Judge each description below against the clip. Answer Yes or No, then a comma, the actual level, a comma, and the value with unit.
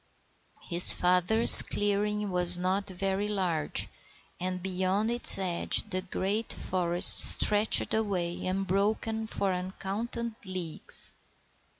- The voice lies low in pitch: No, high, 190 Hz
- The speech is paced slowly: Yes, slow, 100 wpm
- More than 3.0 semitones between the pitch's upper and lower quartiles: No, narrow, 2.4 semitones